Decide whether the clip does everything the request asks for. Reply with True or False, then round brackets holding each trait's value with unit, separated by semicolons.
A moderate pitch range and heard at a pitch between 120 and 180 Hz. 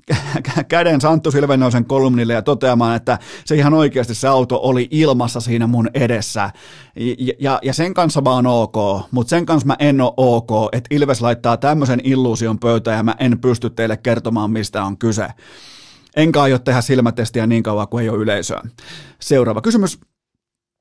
True (3.4 semitones; 125 Hz)